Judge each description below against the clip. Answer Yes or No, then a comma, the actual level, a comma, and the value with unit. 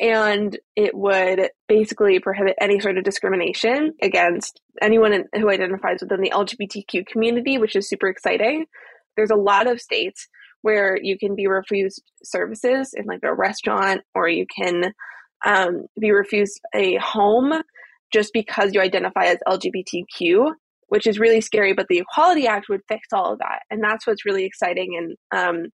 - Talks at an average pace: Yes, average, 165 wpm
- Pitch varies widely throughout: No, average, 2.9 semitones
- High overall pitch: Yes, high, 205 Hz